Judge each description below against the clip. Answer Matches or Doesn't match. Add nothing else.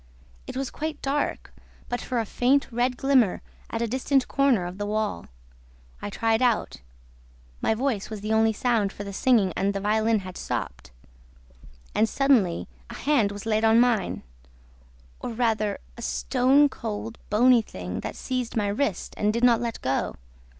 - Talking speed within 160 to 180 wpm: Matches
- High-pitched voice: Matches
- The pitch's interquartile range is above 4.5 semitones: Doesn't match